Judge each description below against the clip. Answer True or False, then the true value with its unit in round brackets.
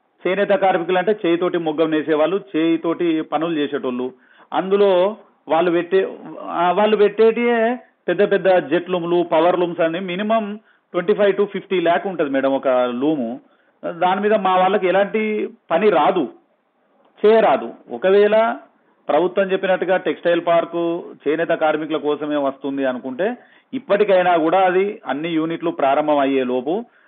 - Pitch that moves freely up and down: False (3.9 semitones)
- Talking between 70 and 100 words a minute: False (125 wpm)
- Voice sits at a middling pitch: True (180 Hz)